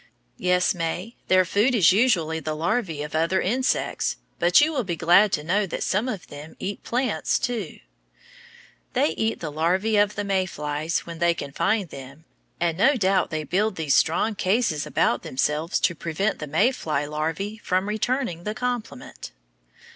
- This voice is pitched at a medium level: Yes, medium, 180 Hz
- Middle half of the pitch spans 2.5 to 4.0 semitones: No, average, 4.9 semitones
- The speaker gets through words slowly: No, average, 175 wpm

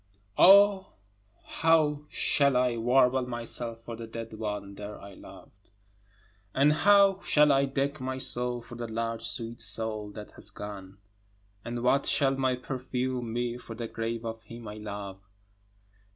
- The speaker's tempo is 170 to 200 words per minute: No, average, 155 wpm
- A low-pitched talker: Yes, low, 120 Hz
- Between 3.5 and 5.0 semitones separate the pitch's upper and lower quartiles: No, average, 3.0 semitones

